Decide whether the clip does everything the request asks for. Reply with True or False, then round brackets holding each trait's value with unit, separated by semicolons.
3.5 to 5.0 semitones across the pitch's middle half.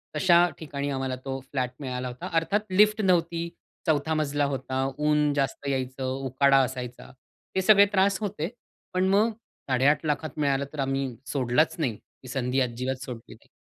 True (4.2 semitones)